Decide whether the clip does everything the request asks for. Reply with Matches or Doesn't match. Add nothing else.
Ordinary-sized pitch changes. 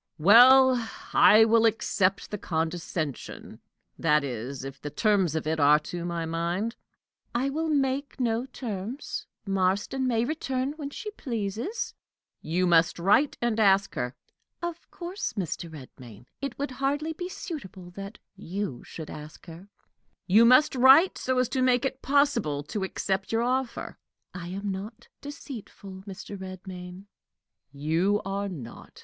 Doesn't match